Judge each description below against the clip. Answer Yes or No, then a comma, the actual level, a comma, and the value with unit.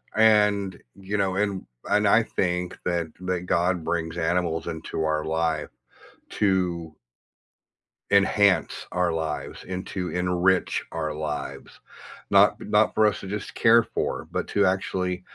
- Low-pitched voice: Yes, very low, 90 Hz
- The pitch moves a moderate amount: Yes, average, 3.1 semitones